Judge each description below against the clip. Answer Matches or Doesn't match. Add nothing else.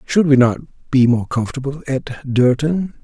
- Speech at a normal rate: Matches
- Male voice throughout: Matches